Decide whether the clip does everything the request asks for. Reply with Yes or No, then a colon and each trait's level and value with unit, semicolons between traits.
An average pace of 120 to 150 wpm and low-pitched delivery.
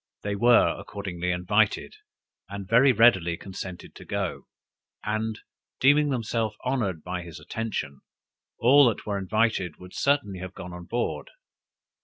Yes: slow, 135 wpm; low, 105 Hz